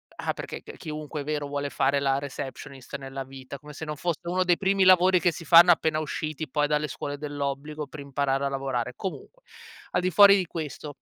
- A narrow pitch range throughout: No, average, 3.2 semitones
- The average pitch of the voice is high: No, medium, 150 Hz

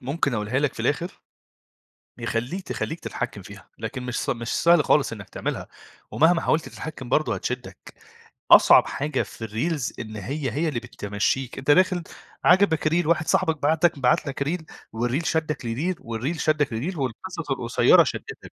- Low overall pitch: No, medium, 145 Hz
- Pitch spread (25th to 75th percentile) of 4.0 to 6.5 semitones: Yes, average, 4.8 semitones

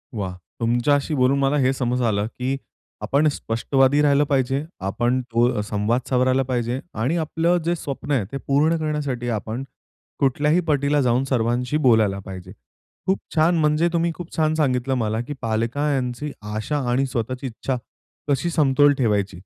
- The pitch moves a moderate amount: Yes, average, 3.7 semitones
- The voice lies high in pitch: No, low, 130 Hz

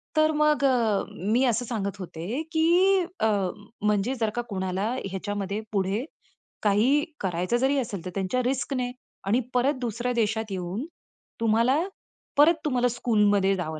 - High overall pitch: Yes, high, 225 Hz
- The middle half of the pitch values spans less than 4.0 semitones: No, average, 4.6 semitones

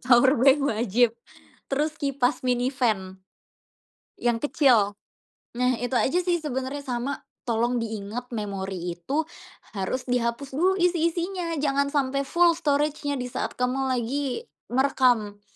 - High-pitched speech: Yes, very high, 255 Hz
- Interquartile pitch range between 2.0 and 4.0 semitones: Yes, average, 3.4 semitones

